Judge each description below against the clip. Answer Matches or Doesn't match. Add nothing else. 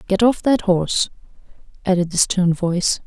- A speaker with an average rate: Matches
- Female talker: Matches